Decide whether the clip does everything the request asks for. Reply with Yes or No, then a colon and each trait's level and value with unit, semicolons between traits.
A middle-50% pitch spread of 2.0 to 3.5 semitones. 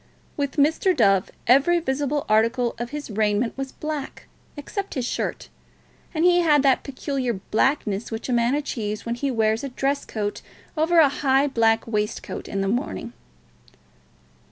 No: average, 4.5 semitones